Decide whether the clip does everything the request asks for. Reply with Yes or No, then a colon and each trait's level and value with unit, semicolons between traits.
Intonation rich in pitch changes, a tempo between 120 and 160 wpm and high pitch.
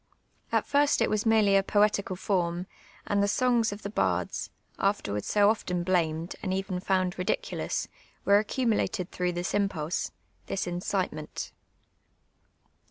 No: narrow, 2.6 semitones; average, 150 wpm; high, 195 Hz